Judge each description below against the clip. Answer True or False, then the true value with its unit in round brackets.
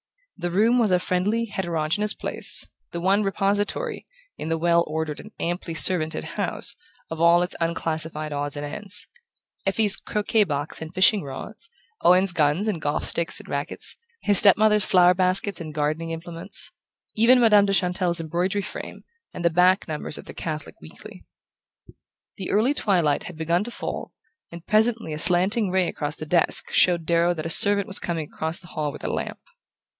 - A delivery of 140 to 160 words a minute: False (175 wpm)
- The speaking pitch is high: False (175 Hz)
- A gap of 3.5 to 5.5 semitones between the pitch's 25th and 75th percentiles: True (3.9 semitones)